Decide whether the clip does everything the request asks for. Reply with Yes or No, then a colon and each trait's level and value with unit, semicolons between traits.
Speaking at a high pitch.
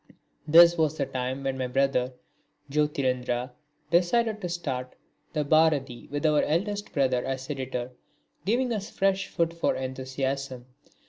No: medium, 140 Hz